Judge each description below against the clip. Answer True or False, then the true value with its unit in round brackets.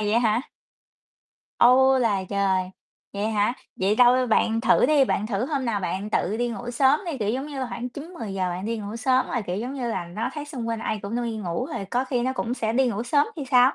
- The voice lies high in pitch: True (235 Hz)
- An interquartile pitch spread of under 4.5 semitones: True (3.8 semitones)